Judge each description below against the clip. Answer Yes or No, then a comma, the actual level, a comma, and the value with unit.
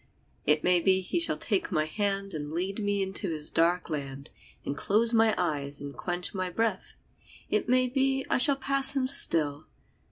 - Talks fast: No, average, 185 wpm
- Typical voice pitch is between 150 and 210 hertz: Yes, high, 190 Hz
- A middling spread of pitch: No, wide, 6.9 semitones